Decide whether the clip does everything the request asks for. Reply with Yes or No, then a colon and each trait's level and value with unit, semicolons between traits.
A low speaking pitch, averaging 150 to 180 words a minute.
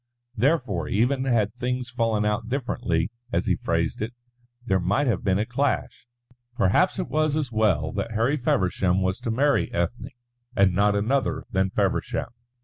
Yes: low, 110 Hz; average, 160 wpm